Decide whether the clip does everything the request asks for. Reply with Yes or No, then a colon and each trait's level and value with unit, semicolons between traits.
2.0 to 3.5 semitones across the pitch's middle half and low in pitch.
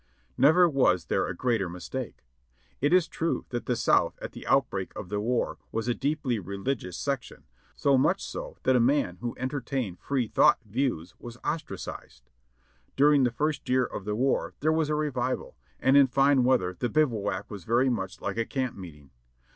No: average, 5.1 semitones; low, 125 Hz